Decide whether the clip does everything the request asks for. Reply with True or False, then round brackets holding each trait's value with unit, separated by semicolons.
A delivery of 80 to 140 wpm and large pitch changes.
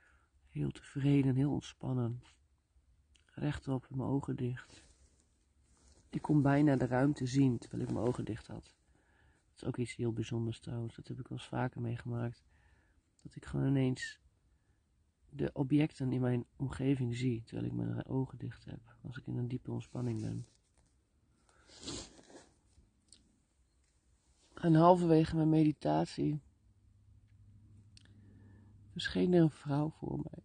True (135 wpm; 8.6 semitones)